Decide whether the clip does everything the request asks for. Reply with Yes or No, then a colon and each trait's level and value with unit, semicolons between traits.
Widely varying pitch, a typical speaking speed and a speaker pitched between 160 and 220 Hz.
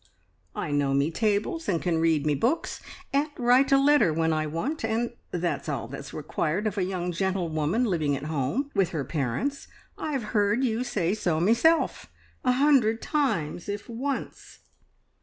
Yes: wide, 8.0 semitones; average, 165 wpm; high, 190 Hz